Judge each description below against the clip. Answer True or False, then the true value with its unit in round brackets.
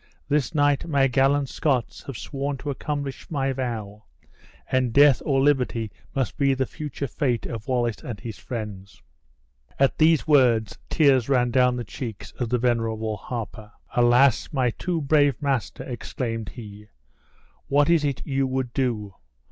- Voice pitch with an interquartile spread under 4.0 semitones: True (3.3 semitones)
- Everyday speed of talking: True (155 wpm)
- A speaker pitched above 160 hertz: False (130 Hz)